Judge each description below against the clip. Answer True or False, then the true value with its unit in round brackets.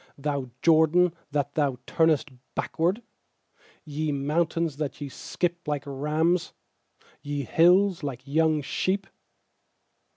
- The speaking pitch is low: False (155 Hz)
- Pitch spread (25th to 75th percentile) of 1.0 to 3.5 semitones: True (2.9 semitones)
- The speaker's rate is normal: False (105 wpm)